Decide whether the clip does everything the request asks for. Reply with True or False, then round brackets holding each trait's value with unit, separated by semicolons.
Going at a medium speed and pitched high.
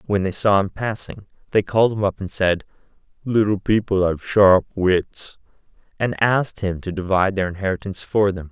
False (175 wpm; 100 Hz)